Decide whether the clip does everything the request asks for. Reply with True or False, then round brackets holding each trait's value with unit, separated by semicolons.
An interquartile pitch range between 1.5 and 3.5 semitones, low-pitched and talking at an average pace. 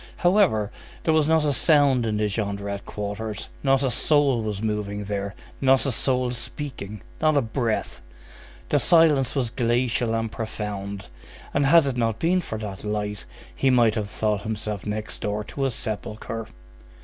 False (4.5 semitones; 115 Hz; 165 wpm)